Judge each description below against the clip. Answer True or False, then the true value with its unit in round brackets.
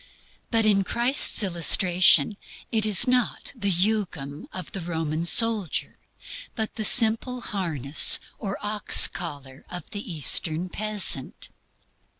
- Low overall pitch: False (195 Hz)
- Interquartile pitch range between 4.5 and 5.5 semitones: True (4.8 semitones)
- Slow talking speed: True (120 wpm)